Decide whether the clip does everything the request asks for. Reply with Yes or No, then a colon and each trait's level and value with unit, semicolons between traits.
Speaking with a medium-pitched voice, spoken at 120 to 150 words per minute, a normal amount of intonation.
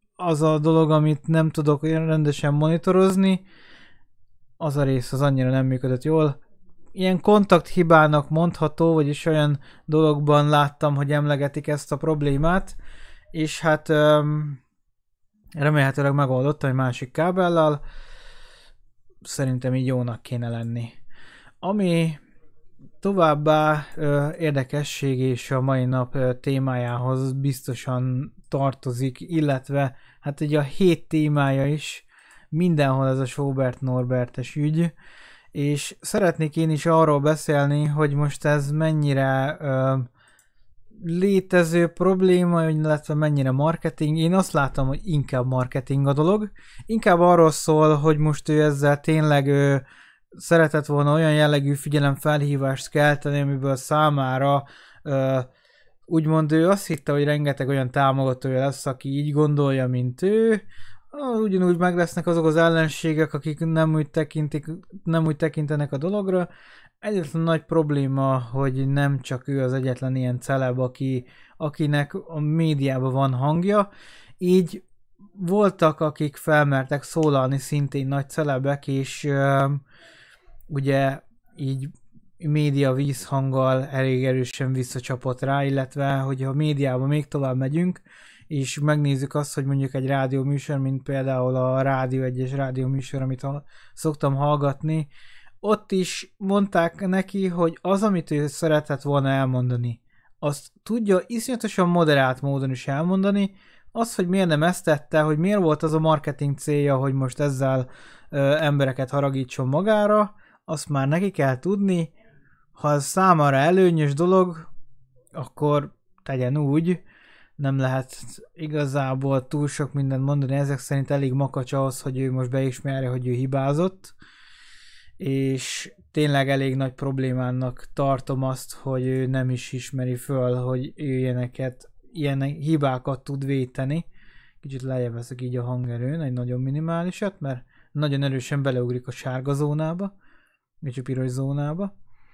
Yes: medium, 145 Hz; average, 130 wpm; average, 3.0 semitones